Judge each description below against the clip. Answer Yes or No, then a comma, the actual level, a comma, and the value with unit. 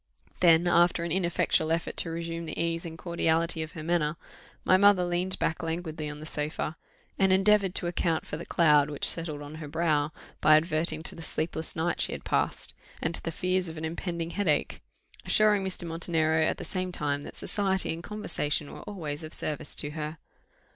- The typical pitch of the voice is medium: Yes, medium, 165 Hz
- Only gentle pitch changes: Yes, narrow, 2.1 semitones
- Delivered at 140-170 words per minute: No, average, 195 wpm